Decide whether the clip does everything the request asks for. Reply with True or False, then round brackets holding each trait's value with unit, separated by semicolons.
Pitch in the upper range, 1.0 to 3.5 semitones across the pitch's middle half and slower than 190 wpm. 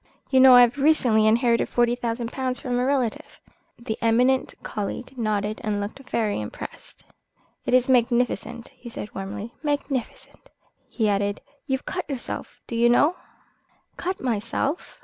True (240 Hz; 3.1 semitones; 150 wpm)